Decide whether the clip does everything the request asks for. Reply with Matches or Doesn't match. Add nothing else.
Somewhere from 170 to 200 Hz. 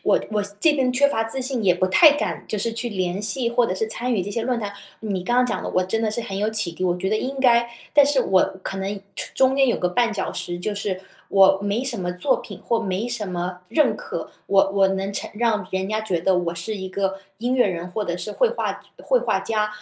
Doesn't match